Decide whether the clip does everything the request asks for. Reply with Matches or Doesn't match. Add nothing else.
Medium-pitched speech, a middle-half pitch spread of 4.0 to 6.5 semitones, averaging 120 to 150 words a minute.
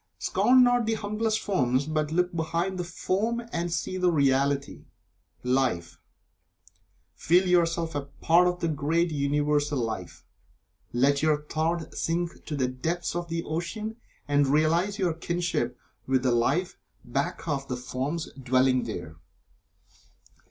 Matches